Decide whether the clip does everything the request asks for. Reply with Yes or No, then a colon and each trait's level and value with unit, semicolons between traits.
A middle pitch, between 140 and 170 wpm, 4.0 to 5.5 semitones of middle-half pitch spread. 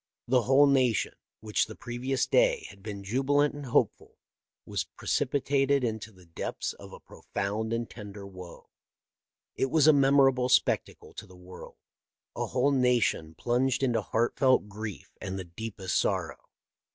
No: low, 120 Hz; average, 150 wpm; average, 4.8 semitones